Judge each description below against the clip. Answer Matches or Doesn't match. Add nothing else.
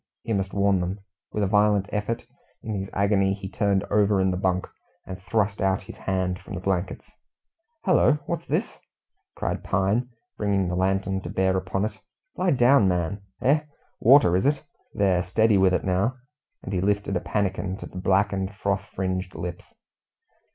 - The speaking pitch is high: Doesn't match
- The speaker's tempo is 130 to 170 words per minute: Doesn't match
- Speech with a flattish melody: Matches